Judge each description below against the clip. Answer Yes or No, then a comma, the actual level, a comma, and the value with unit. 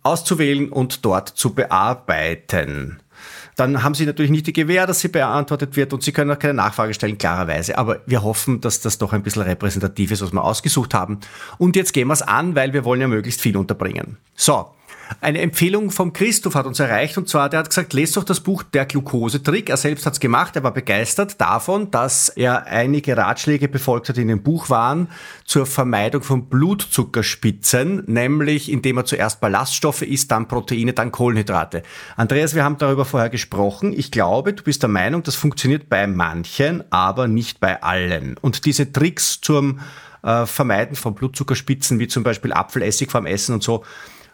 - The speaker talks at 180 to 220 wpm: Yes, fast, 190 wpm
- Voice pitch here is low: Yes, low, 130 Hz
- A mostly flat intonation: No, average, 4.8 semitones